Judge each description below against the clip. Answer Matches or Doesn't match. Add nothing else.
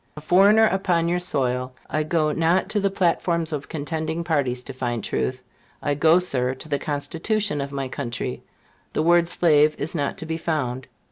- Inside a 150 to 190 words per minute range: Matches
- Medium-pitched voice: Matches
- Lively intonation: Doesn't match